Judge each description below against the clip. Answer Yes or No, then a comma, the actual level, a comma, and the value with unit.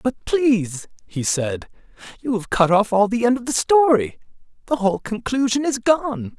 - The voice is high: Yes, high, 215 Hz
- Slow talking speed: No, average, 180 wpm